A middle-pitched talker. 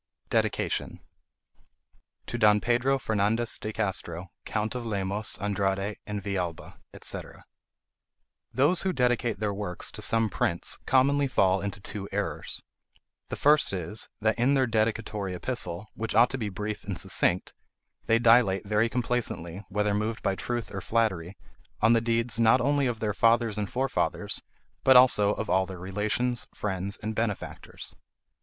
No: low, 110 Hz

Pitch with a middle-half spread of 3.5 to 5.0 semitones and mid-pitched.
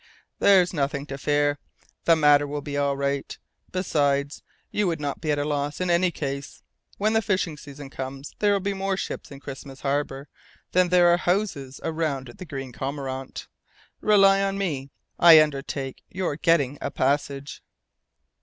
Yes: average, 4.3 semitones; medium, 145 Hz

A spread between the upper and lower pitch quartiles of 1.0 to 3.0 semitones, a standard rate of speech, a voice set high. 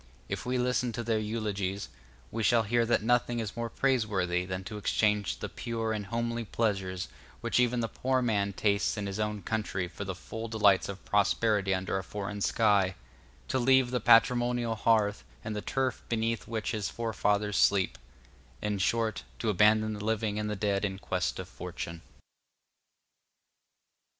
No: narrow, 2.4 semitones; average, 170 wpm; low, 110 Hz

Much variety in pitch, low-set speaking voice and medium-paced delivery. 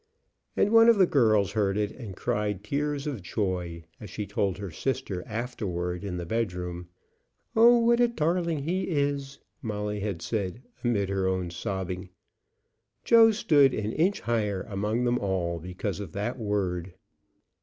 Yes: wide, 6.7 semitones; low, 105 Hz; average, 155 wpm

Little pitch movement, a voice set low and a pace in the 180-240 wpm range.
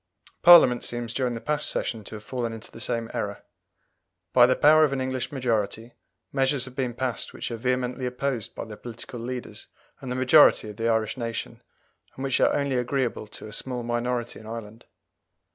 Yes: narrow, 2.2 semitones; low, 125 Hz; average, 195 wpm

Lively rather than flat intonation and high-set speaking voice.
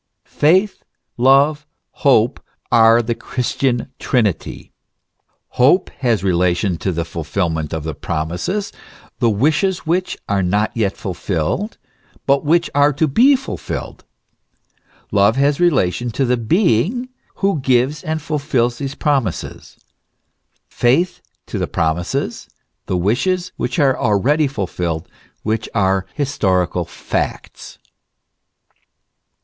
No: wide, 7.5 semitones; low, 120 Hz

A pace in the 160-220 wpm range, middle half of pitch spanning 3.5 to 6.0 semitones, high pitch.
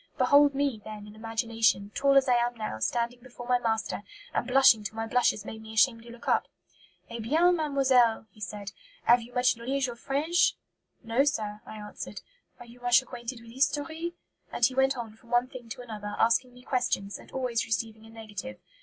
No: average, 200 wpm; average, 2.8 semitones; high, 240 Hz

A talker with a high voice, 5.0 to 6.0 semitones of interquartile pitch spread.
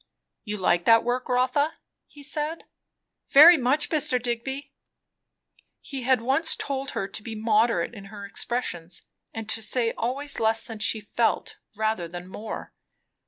No: high, 235 Hz; average, 3.8 semitones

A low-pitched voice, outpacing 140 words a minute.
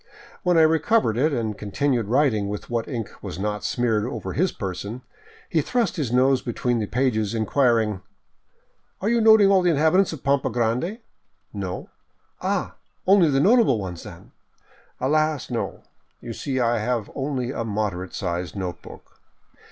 Yes: low, 125 Hz; average, 175 wpm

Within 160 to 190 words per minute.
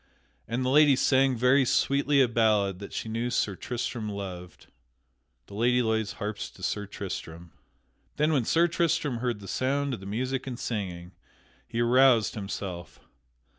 Yes: average, 165 wpm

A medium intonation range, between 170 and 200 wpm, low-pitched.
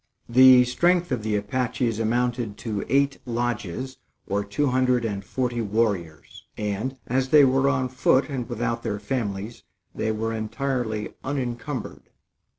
No: average, 3.2 semitones; average, 140 wpm; low, 120 Hz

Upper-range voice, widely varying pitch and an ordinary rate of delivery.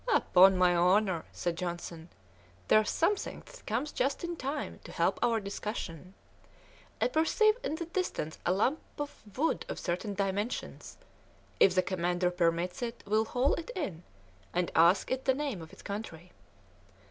Yes: high, 200 Hz; wide, 7.4 semitones; average, 160 wpm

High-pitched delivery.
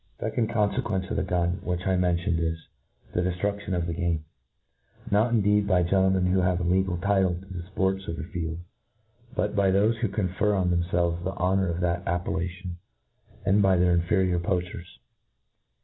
No: very low, 90 Hz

